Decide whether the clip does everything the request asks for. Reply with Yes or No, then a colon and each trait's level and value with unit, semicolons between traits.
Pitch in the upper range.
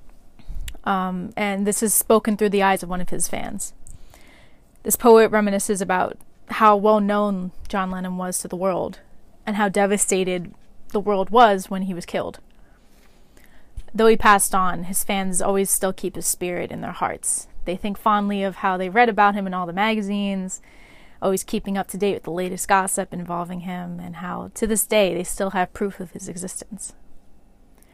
Yes: high, 195 Hz